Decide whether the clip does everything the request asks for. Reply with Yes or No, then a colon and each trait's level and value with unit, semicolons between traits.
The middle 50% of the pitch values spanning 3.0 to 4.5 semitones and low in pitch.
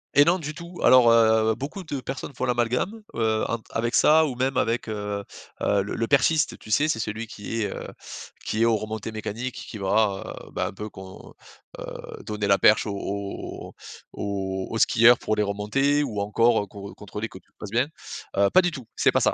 Yes: average, 3.8 semitones; low, 110 Hz